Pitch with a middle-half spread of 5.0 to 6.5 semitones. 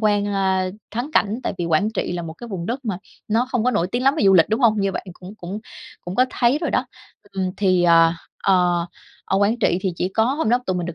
No: average, 4.2 semitones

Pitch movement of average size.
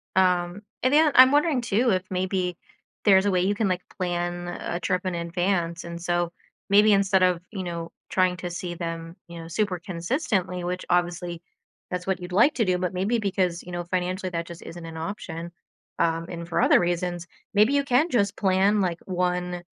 No: narrow, 2.2 semitones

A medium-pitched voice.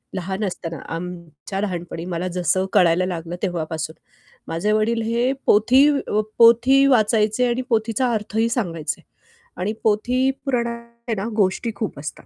No: high, 210 Hz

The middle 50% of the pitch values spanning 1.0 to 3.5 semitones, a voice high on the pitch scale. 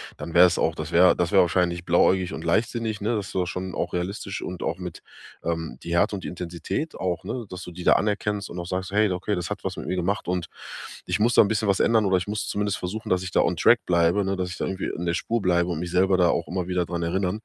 No: narrow, 2.5 semitones; very low, 90 Hz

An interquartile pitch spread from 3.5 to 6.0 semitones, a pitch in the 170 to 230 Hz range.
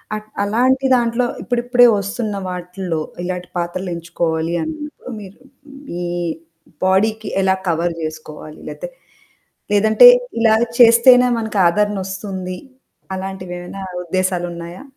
Yes: average, 4.3 semitones; high, 190 Hz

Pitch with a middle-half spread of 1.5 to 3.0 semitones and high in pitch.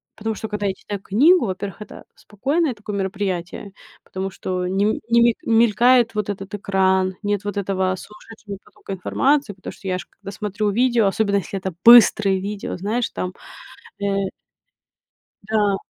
Yes: narrow, 2.5 semitones; high, 205 Hz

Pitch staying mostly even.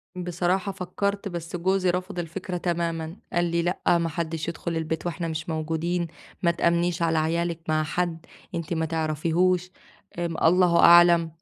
Yes: narrow, 1.5 semitones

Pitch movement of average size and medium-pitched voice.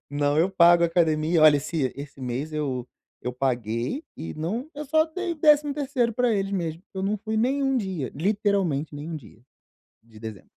No: wide, 8.4 semitones; medium, 170 Hz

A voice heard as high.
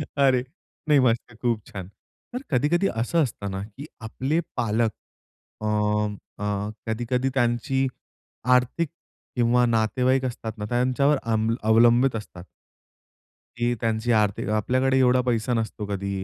No: low, 120 Hz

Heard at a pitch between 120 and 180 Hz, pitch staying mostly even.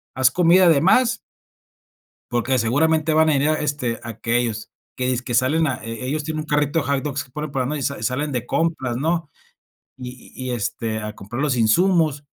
No: medium, 140 Hz; average, 4.3 semitones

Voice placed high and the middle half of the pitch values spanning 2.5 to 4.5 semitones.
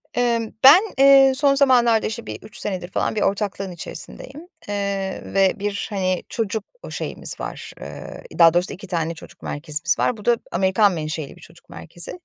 No: high, 200 Hz; average, 5.0 semitones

